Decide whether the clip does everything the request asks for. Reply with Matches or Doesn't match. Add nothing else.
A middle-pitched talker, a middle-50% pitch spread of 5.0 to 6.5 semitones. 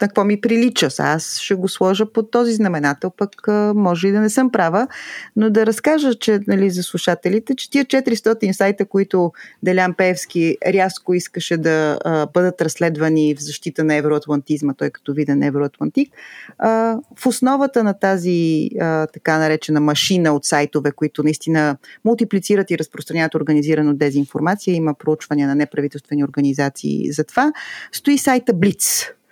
Matches